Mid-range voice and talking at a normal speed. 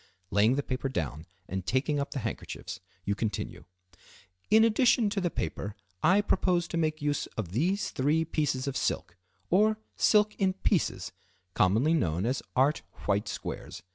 Yes: medium, 145 Hz; average, 160 wpm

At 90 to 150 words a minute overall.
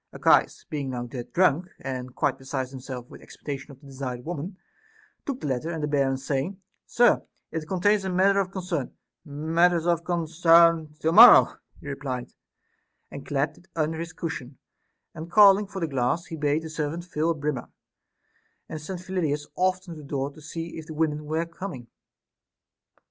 No: average, 180 wpm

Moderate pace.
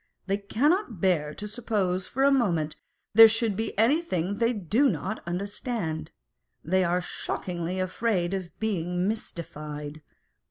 No: slow, 130 wpm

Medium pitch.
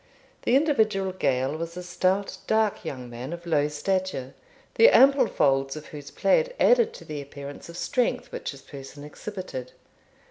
Yes: medium, 170 Hz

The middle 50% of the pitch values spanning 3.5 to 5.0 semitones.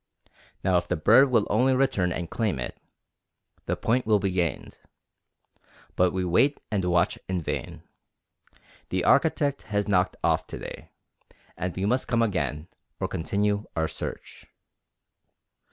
Yes: average, 4.4 semitones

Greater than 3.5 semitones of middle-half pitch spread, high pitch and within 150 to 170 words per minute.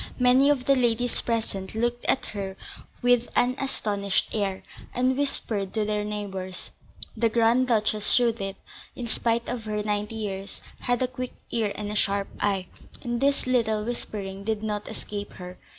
No: average, 3.1 semitones; high, 220 Hz; average, 165 wpm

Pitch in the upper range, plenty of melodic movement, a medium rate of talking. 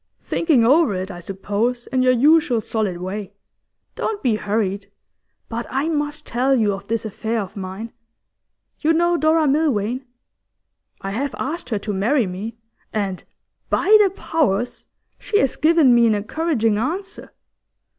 Yes: high, 235 Hz; wide, 6.5 semitones; average, 150 wpm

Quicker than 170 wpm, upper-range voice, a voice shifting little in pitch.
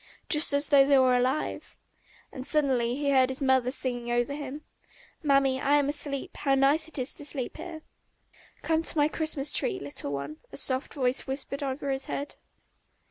Yes: average, 190 wpm; very high, 275 Hz; narrow, 2.1 semitones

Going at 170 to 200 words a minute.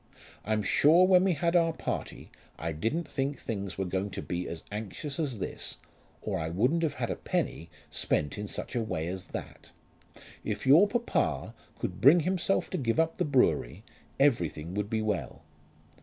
Yes: average, 180 wpm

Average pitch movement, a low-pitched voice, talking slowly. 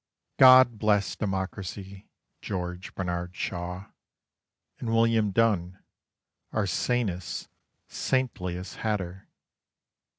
Yes: average, 3.8 semitones; very low, 95 Hz; slow, 80 wpm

